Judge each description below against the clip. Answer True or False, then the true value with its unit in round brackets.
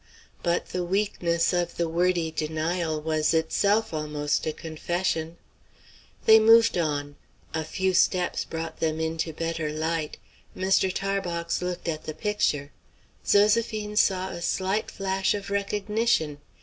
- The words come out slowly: True (130 wpm)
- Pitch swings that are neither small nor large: True (3.6 semitones)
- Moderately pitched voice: True (170 Hz)